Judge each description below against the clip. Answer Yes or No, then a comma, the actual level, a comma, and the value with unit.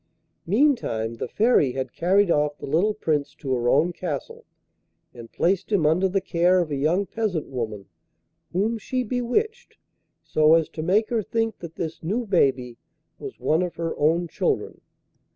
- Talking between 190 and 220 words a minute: No, average, 170 wpm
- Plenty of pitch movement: Yes, wide, 6.1 semitones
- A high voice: No, medium, 170 Hz